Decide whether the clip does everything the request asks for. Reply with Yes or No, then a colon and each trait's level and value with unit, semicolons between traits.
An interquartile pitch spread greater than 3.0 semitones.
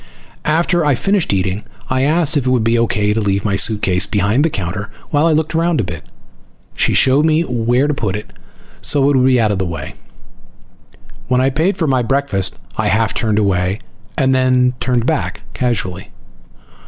Yes: wide, 5.6 semitones